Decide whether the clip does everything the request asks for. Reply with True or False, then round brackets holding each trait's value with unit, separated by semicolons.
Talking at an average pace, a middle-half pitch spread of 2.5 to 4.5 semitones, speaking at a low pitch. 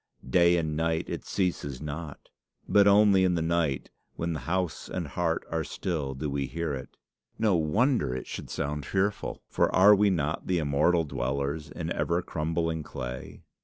True (165 wpm; 3.6 semitones; 80 Hz)